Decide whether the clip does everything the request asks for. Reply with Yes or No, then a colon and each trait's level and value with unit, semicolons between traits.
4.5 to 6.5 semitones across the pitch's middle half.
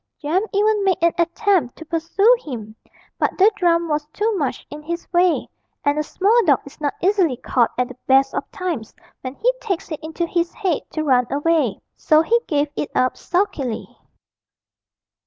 Yes: average, 4.8 semitones